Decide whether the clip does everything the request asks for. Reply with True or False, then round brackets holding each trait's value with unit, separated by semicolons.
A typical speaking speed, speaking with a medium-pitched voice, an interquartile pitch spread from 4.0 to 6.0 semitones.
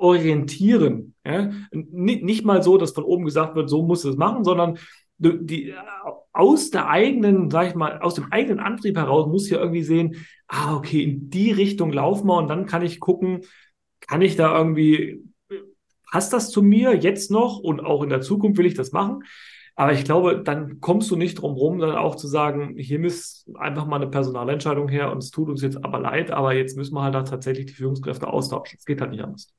False (220 wpm; 165 Hz; 4.4 semitones)